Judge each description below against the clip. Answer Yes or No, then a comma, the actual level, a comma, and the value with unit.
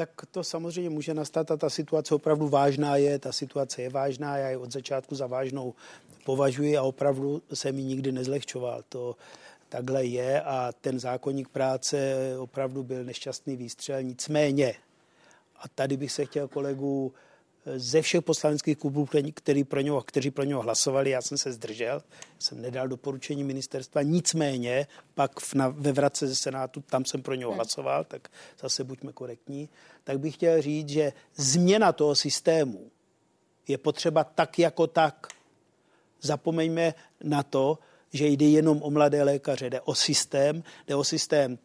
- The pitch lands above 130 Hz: Yes, medium, 140 Hz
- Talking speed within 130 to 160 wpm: Yes, average, 155 wpm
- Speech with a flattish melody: Yes, narrow, 2.2 semitones